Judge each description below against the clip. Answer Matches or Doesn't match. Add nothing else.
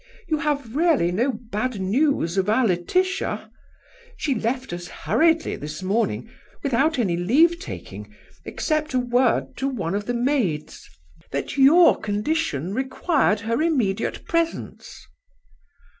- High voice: Matches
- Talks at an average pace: Doesn't match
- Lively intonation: Matches